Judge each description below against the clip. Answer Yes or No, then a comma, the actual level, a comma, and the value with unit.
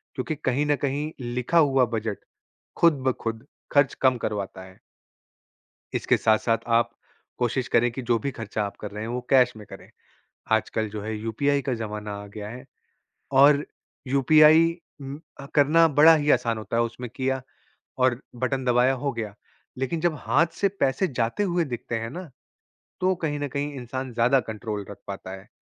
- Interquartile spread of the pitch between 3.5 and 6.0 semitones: Yes, average, 4.1 semitones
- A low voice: Yes, low, 125 Hz